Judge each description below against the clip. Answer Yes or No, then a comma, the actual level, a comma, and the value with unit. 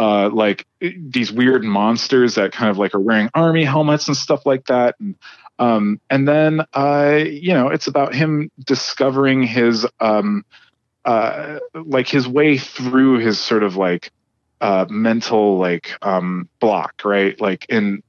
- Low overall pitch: Yes, low, 125 Hz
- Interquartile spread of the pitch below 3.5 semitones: No, wide, 5.4 semitones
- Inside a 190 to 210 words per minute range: No, average, 160 wpm